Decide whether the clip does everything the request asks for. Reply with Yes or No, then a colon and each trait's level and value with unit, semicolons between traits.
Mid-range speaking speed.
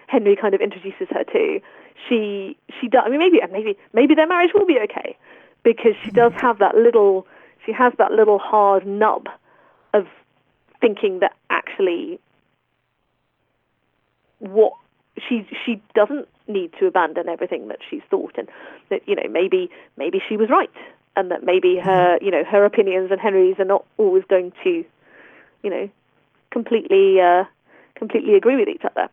Yes: average, 165 wpm